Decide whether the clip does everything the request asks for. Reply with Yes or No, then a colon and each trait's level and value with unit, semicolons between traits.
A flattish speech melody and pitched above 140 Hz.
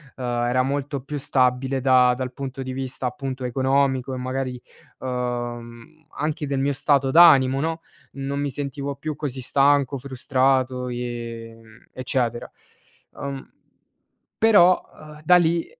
No: narrow, 2.0 semitones; low, 135 Hz